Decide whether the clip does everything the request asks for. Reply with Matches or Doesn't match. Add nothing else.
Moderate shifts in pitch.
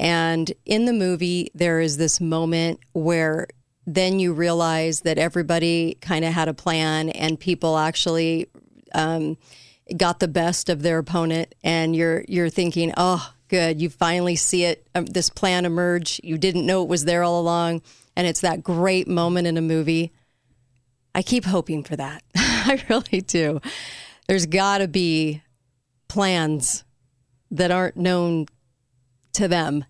Doesn't match